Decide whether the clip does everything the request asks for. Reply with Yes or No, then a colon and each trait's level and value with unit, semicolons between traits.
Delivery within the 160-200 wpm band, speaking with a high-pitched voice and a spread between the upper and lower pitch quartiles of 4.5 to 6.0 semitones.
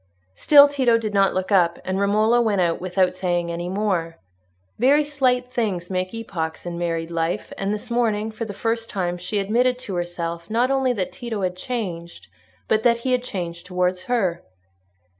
Yes: average, 180 wpm; high, 200 Hz; average, 5.0 semitones